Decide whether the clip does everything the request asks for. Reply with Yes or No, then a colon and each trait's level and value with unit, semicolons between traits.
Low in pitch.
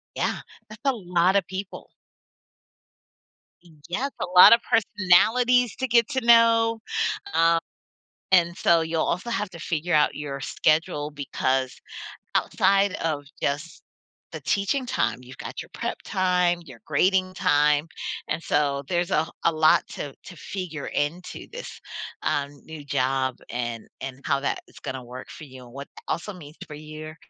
No: medium, 165 Hz